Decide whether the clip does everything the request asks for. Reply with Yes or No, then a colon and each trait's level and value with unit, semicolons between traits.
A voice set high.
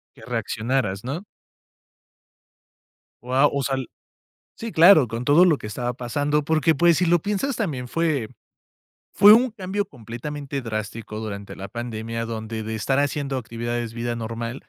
No: low, 130 Hz